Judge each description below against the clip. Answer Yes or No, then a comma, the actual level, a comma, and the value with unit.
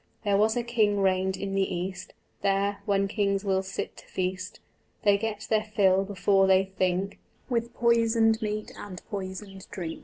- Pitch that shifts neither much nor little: No, narrow, 2.1 semitones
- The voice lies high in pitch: Yes, high, 200 Hz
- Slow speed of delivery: No, average, 165 wpm